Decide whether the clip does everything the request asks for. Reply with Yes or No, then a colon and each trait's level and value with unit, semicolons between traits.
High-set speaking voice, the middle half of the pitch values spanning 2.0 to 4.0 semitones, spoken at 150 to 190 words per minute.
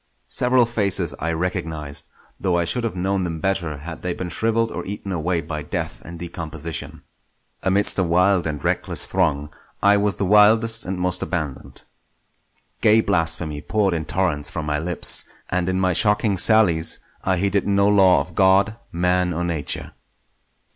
No: very low, 90 Hz; average, 3.4 semitones; average, 165 wpm